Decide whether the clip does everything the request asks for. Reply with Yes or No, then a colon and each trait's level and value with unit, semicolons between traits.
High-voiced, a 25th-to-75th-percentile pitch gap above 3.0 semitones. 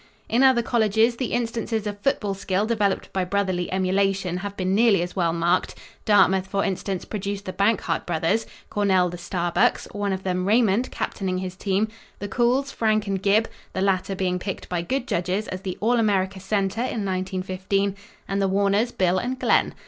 No: high, 195 Hz; narrow, 2.6 semitones